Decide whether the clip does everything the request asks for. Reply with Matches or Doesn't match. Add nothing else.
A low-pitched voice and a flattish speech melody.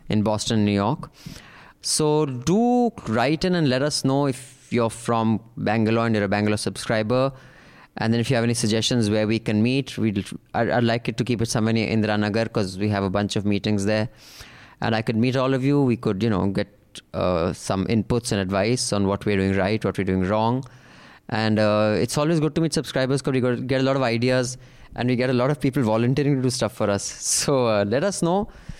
Doesn't match